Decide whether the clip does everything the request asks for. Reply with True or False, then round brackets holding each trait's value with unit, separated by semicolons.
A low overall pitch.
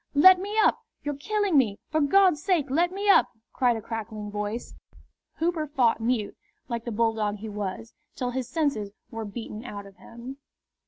False (245 Hz)